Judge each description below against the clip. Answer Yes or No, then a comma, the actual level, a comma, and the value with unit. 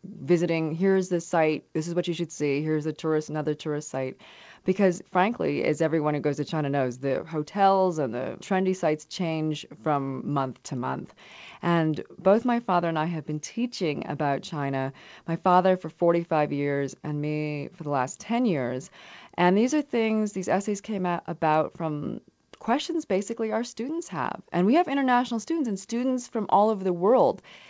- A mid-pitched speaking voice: Yes, medium, 170 Hz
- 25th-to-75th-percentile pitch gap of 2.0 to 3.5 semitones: No, average, 4.7 semitones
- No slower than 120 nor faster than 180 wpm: No, average, 190 wpm